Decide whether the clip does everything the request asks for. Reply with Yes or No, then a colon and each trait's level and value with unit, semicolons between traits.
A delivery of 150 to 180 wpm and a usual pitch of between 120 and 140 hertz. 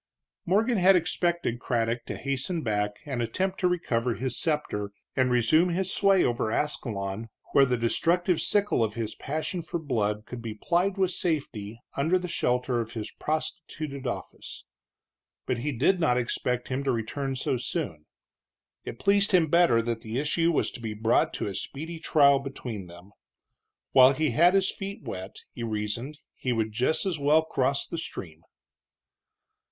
Yes: average, 170 wpm; low, 135 Hz